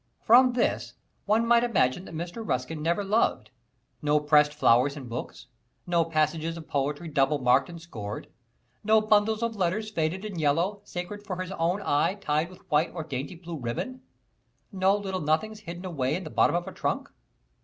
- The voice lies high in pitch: No, medium, 170 Hz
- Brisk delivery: No, average, 180 wpm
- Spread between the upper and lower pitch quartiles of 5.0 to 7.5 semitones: Yes, average, 5.3 semitones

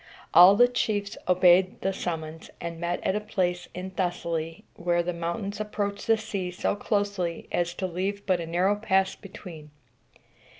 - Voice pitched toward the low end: No, medium, 185 Hz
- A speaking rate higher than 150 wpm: Yes, average, 165 wpm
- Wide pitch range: No, average, 2.7 semitones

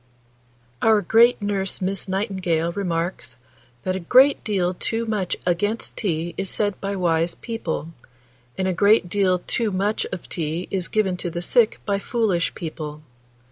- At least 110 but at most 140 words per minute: No, average, 155 wpm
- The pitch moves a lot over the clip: No, average, 3.3 semitones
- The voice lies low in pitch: No, high, 190 Hz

